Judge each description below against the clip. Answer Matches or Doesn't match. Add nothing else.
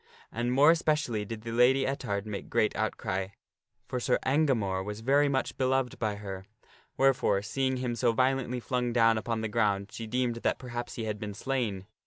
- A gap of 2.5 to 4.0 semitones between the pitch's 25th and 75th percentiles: Matches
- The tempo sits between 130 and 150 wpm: Doesn't match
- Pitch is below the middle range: Matches